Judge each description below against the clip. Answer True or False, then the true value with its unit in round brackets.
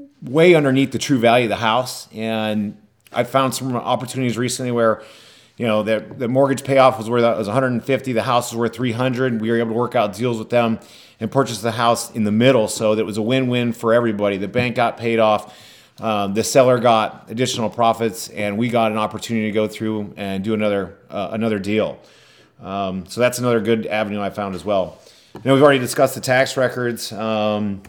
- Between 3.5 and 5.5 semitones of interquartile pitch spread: False (2.5 semitones)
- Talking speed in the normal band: False (210 wpm)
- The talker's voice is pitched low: True (115 Hz)